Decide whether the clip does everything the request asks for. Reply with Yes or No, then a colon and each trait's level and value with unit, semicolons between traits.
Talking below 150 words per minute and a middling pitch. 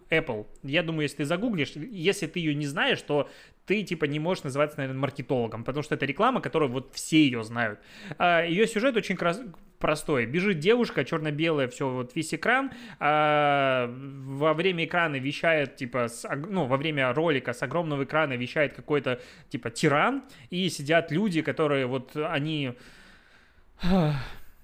No: average, 155 wpm; medium, 150 Hz